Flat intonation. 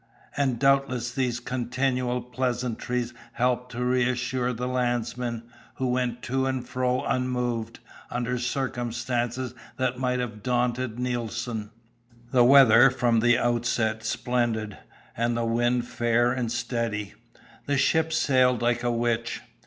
Yes: narrow, 1.2 semitones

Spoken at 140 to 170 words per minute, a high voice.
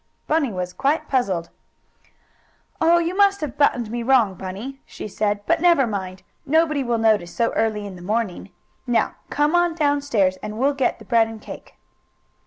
No: average, 180 wpm; high, 235 Hz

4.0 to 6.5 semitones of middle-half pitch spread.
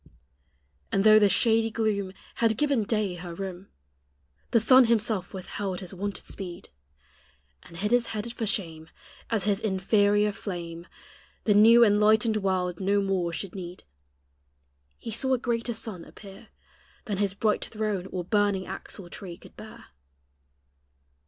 No: average, 2.7 semitones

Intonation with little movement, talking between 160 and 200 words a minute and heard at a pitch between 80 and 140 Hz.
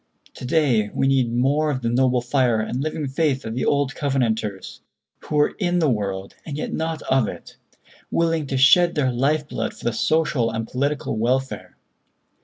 No: average, 4.1 semitones; average, 185 wpm; low, 135 Hz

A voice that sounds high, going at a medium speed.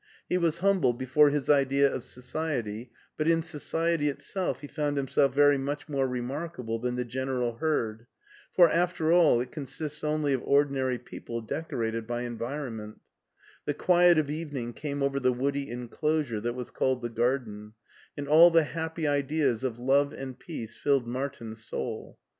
No: medium, 140 Hz; average, 170 wpm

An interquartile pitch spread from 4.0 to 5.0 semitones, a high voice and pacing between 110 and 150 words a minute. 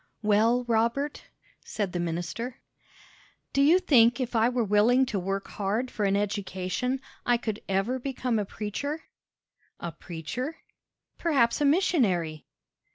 Yes: average, 4.6 semitones; high, 230 Hz; slow, 135 wpm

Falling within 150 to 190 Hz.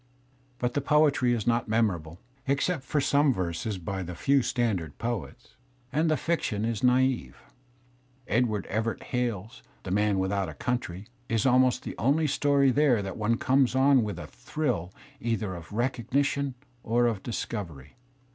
No: low, 120 Hz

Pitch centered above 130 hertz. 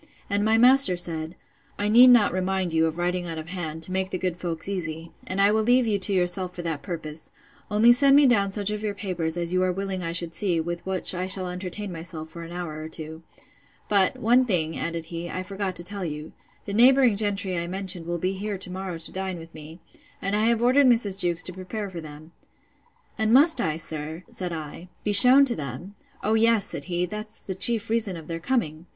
Yes: medium, 185 Hz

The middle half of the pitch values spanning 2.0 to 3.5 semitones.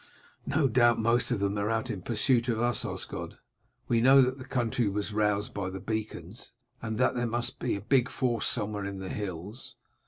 Yes: average, 3.0 semitones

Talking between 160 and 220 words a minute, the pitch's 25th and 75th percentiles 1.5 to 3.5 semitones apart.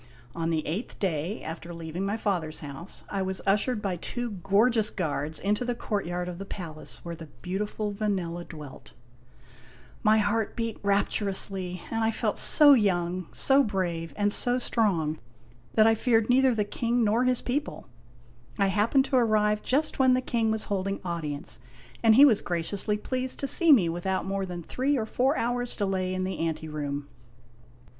No: average, 175 wpm; average, 4.8 semitones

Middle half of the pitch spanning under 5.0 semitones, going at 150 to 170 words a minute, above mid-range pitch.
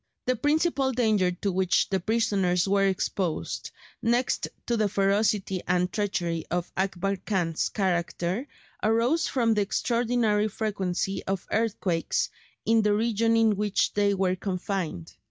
No: average, 3.4 semitones; slow, 135 wpm; high, 200 Hz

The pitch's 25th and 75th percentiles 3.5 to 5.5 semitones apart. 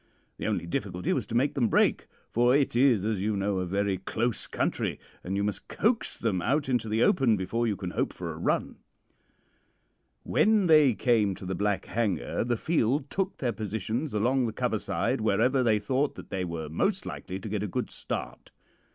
Yes: average, 4.8 semitones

